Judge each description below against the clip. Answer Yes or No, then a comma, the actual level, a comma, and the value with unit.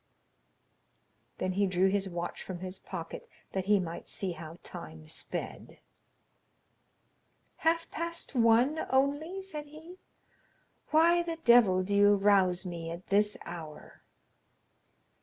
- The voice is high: Yes, high, 200 Hz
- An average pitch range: No, wide, 8.5 semitones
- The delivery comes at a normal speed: No, slow, 120 wpm